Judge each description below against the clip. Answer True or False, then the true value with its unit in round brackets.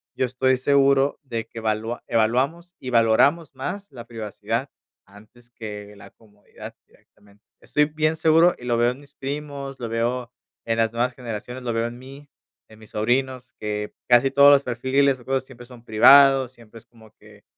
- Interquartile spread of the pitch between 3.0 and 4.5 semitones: True (3.3 semitones)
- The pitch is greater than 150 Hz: False (125 Hz)